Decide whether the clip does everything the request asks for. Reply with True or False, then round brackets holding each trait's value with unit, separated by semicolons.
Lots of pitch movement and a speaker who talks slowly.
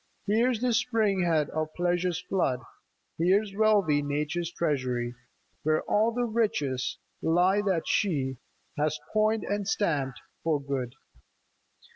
True (6.1 semitones; 130 wpm)